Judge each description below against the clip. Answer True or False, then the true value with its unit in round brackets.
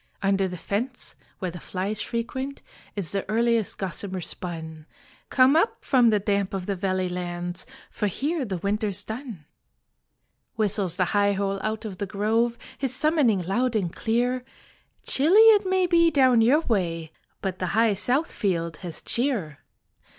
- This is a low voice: False (205 Hz)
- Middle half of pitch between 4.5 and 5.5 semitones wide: True (5.1 semitones)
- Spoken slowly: False (160 wpm)